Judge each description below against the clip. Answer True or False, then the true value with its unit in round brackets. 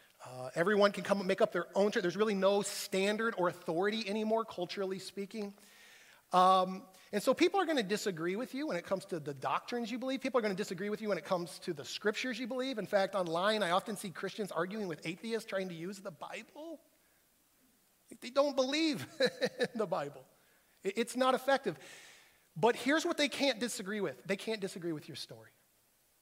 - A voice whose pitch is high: True (205 Hz)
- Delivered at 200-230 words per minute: True (205 wpm)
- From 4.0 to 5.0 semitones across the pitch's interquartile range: True (4.5 semitones)